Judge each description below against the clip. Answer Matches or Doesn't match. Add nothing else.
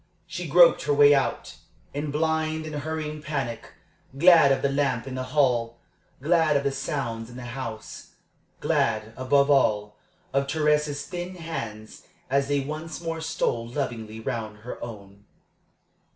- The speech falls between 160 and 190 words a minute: Doesn't match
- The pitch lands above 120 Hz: Matches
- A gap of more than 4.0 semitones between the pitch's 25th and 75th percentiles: Matches